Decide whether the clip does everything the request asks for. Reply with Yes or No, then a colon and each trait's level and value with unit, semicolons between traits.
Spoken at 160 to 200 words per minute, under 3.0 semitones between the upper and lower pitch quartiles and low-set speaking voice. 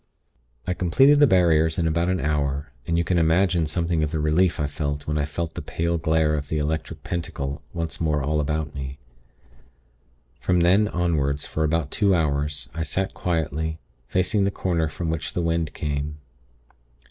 Yes: average, 180 wpm; narrow, 2.5 semitones; very low, 80 Hz